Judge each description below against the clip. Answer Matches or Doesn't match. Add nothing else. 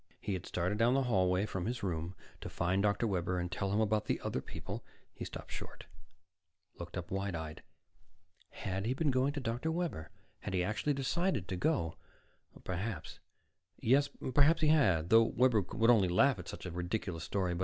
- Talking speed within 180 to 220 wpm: Matches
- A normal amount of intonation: Doesn't match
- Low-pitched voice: Matches